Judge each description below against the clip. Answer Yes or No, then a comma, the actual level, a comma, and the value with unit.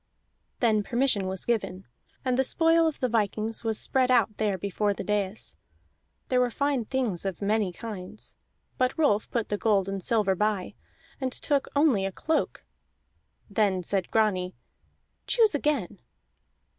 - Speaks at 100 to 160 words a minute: Yes, average, 150 wpm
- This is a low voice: No, high, 215 Hz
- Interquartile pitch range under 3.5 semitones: No, average, 4.4 semitones